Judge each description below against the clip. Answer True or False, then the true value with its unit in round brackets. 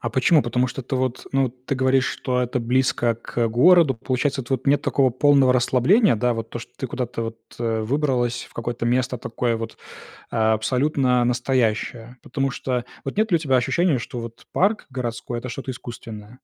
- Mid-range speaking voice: False (125 Hz)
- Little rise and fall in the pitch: True (2.2 semitones)